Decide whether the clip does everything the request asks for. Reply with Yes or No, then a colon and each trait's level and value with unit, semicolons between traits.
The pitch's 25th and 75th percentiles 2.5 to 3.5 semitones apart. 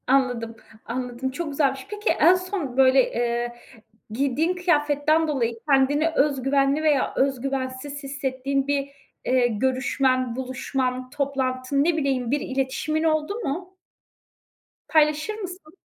Yes: average, 2.9 semitones